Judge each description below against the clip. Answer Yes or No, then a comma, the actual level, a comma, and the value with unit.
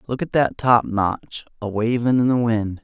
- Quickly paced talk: No, average, 190 wpm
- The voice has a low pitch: Yes, low, 115 Hz